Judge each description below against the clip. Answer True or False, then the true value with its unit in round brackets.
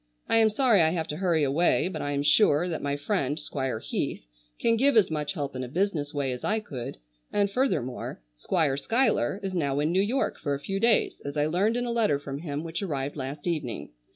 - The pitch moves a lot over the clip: True (5.8 semitones)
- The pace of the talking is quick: True (230 wpm)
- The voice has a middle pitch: True (155 Hz)